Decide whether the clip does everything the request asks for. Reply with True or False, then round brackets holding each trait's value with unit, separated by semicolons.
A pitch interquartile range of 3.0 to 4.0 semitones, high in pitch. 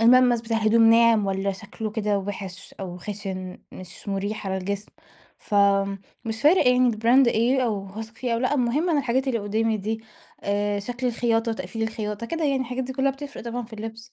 True (3.3 semitones; 225 Hz)